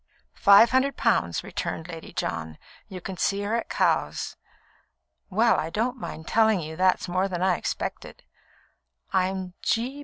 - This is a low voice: No, high, 190 Hz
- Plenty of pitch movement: No, average, 4.3 semitones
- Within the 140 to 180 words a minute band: Yes, average, 150 wpm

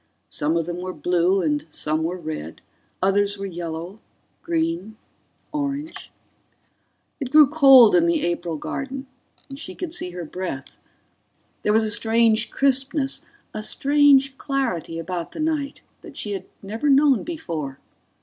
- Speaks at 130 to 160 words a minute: Yes, average, 145 wpm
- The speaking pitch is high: Yes, high, 205 Hz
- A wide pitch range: Yes, wide, 8.2 semitones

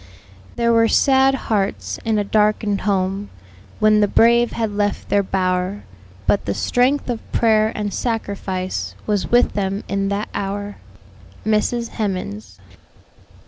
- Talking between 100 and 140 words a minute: Yes, slow, 135 wpm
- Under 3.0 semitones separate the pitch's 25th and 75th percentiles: Yes, narrow, 2.6 semitones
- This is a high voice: Yes, high, 205 Hz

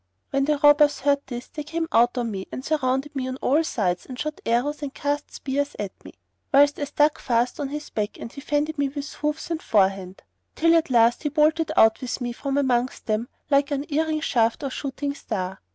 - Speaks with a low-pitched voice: No, very high, 280 Hz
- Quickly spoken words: Yes, fast, 215 wpm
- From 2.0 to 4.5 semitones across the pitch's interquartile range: Yes, average, 3.5 semitones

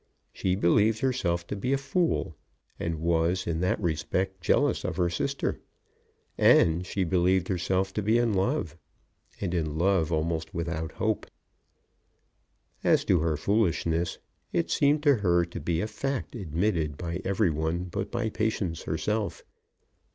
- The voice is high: No, very low, 90 Hz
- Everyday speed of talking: Yes, average, 150 wpm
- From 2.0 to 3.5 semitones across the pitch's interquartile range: No, average, 4.1 semitones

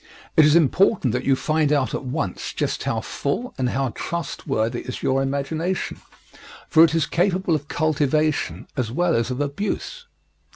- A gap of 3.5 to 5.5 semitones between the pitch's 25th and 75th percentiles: Yes, average, 3.9 semitones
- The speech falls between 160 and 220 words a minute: Yes, average, 165 wpm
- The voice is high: No, medium, 150 Hz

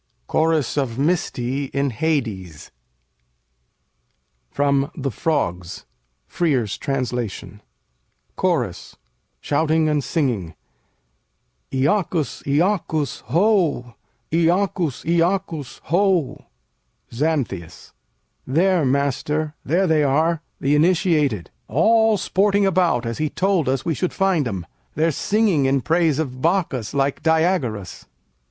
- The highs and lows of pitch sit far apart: No, average, 4.7 semitones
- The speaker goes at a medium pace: No, slow, 100 wpm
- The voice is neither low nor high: Yes, medium, 150 Hz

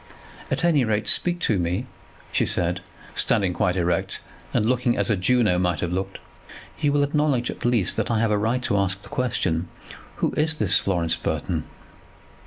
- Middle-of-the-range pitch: No, low, 105 Hz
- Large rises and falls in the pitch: Yes, wide, 5.8 semitones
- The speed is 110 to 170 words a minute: No, average, 185 wpm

